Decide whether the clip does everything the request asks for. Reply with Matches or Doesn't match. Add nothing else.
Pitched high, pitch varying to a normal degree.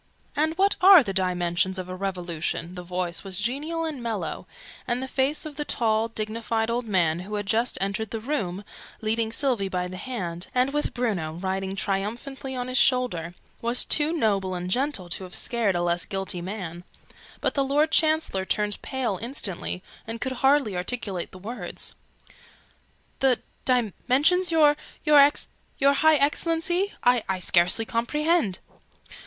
Doesn't match